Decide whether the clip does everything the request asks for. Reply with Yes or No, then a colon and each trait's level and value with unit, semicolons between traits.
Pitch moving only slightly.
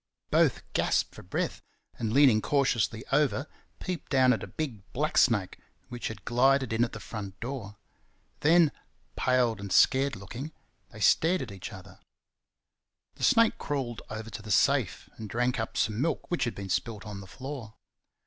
No: average, 4.4 semitones